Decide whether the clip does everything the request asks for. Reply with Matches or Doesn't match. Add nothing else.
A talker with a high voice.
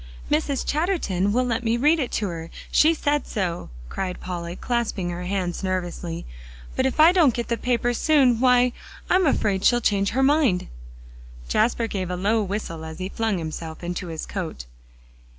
Matches